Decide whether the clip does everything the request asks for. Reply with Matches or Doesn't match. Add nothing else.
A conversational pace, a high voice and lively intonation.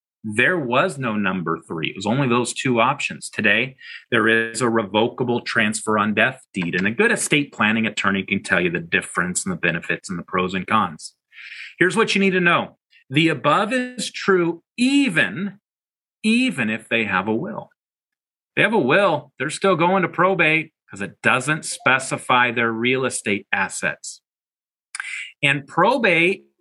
Doesn't match